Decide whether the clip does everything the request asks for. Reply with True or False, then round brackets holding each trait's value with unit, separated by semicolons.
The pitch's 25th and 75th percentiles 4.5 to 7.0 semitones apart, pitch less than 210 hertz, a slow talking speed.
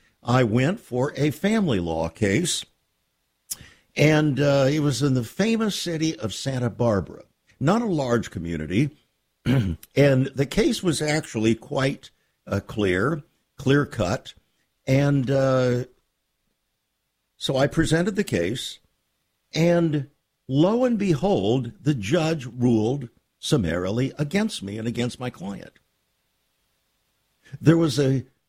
True (4.8 semitones; 135 Hz; 120 wpm)